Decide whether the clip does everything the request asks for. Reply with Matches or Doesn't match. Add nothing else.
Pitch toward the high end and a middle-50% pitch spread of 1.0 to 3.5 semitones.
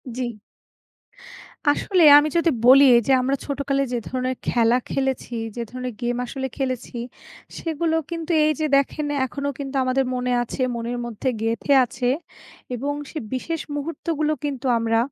Matches